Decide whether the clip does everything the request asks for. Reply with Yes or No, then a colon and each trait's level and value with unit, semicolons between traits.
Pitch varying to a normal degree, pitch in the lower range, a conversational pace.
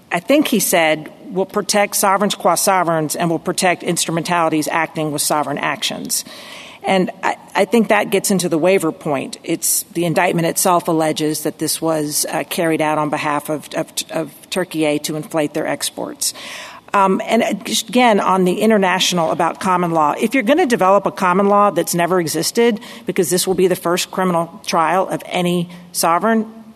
No: average, 4.2 semitones; medium, 180 Hz; average, 180 wpm